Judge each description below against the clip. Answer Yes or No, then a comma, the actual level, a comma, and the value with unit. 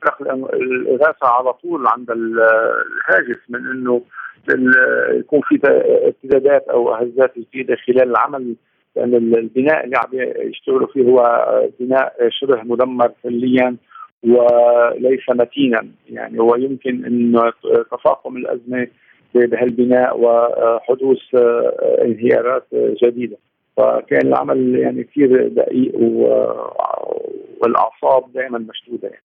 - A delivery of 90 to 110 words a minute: Yes, average, 95 wpm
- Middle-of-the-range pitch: No, low, 125 Hz